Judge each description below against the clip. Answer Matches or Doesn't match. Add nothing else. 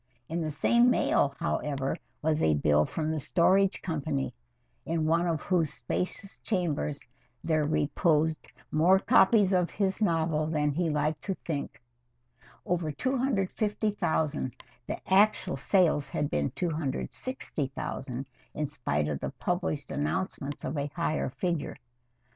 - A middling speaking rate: Doesn't match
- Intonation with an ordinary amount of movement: Matches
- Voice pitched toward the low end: Doesn't match